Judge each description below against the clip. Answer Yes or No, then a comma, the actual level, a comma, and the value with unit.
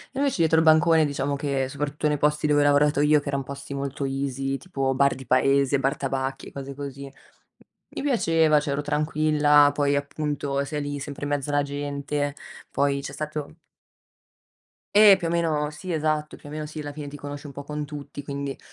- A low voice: No, medium, 145 Hz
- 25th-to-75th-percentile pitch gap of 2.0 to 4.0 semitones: No, narrow, 1.4 semitones